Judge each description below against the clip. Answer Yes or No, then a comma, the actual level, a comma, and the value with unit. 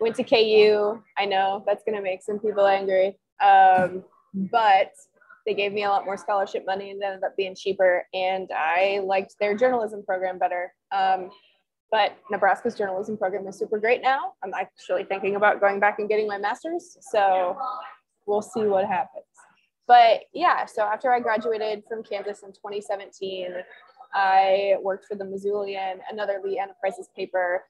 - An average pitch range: No, narrow, 2.1 semitones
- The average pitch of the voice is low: No, high, 200 Hz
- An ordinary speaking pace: Yes, average, 165 wpm